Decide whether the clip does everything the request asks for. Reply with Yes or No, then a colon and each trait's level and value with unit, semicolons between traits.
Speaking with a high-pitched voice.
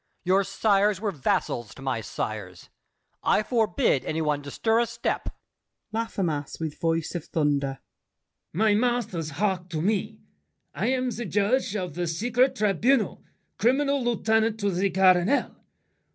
Yes: high, 195 Hz